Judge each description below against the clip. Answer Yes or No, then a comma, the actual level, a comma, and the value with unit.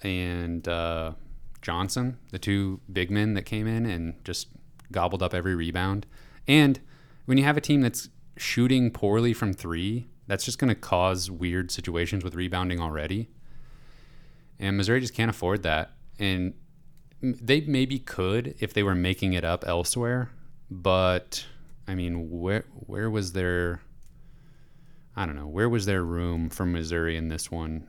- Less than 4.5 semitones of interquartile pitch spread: No, average, 5.2 semitones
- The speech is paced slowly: No, average, 155 wpm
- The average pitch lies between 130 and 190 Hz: No, very low, 95 Hz